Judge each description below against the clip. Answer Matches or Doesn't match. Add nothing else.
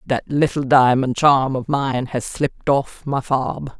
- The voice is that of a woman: Matches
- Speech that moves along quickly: Doesn't match